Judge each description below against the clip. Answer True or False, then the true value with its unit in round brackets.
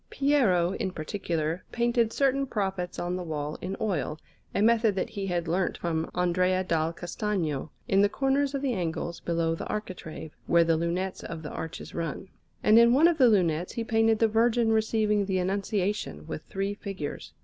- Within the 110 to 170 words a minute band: False (180 wpm)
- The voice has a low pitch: False (190 Hz)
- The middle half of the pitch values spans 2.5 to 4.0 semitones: False (4.7 semitones)